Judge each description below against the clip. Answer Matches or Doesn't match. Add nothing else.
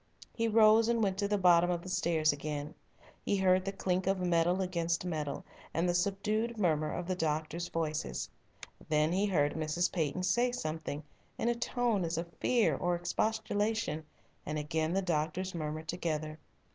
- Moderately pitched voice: Matches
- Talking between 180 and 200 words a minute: Doesn't match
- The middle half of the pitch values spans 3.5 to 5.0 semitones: Matches